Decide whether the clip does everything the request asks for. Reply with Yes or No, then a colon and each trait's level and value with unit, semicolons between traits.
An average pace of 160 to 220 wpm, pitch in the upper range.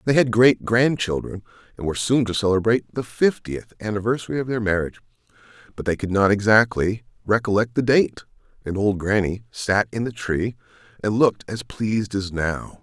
No: average, 175 wpm; low, 110 Hz